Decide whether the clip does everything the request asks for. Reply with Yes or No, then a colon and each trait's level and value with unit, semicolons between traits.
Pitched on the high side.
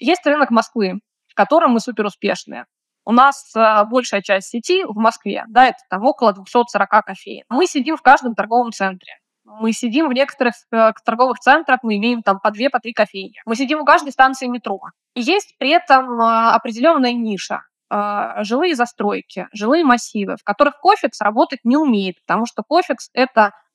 Yes: high, 240 Hz